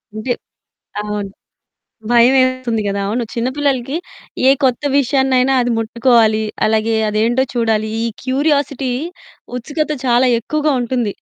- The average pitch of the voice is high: Yes, high, 245 Hz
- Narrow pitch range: No, average, 3.0 semitones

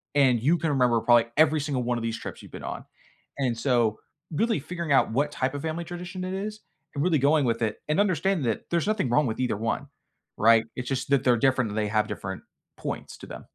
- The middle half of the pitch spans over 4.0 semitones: Yes, wide, 5.4 semitones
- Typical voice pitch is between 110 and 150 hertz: Yes, low, 135 Hz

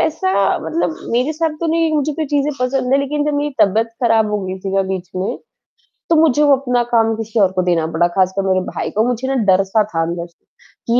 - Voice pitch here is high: Yes, high, 230 Hz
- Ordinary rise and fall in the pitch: No, wide, 7.1 semitones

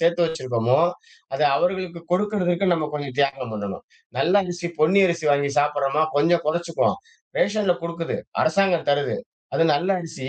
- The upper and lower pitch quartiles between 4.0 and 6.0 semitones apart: No, average, 3.6 semitones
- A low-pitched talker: No, medium, 165 Hz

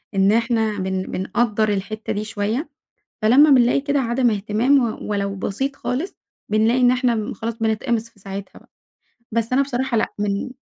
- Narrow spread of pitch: No, average, 3.3 semitones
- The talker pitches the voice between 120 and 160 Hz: No, high, 225 Hz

